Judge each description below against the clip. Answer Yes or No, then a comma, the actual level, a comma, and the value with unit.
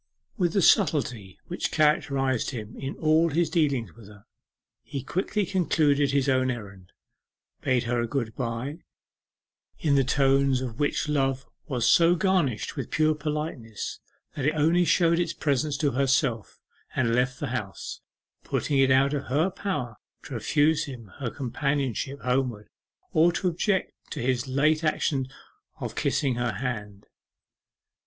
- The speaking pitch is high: No, low, 135 Hz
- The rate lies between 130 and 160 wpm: Yes, average, 150 wpm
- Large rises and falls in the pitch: No, average, 4.0 semitones